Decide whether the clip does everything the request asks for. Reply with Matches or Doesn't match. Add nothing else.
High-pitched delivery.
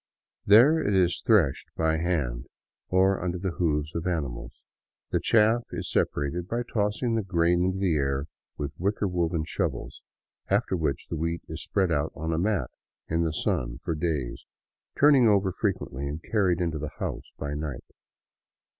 Doesn't match